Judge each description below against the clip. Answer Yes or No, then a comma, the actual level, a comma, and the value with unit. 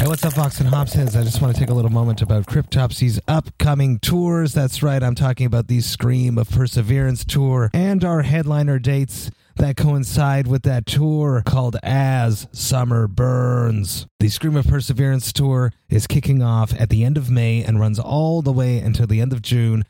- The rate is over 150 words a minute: Yes, average, 195 wpm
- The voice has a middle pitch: No, low, 130 Hz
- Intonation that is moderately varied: Yes, average, 3.2 semitones